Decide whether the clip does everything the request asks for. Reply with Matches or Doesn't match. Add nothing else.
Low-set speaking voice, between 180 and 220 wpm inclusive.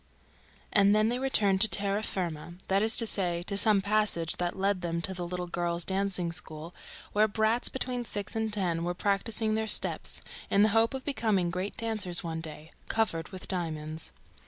Doesn't match